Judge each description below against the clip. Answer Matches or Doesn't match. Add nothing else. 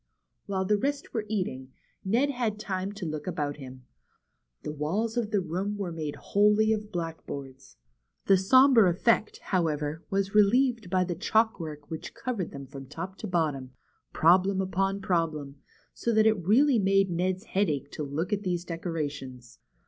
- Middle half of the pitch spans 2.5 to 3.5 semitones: Doesn't match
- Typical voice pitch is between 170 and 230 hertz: Matches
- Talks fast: Doesn't match